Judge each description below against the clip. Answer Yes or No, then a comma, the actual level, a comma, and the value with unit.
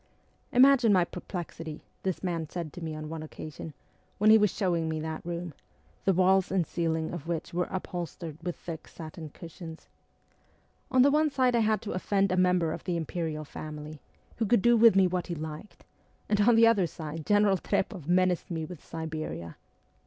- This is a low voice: No, medium, 175 Hz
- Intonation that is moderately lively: Yes, average, 3.6 semitones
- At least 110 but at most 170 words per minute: No, average, 190 wpm